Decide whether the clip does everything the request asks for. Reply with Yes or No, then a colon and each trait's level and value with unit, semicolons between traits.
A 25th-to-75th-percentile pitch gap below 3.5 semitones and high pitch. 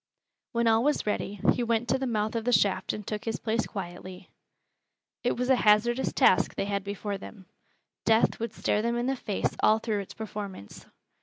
Yes: narrow, 2.6 semitones; high, 220 Hz